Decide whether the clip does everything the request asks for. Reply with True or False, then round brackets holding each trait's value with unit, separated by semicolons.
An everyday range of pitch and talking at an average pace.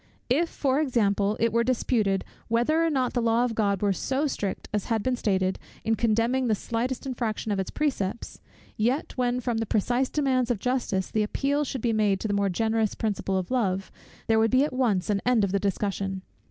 False (4.0 semitones; 210 wpm)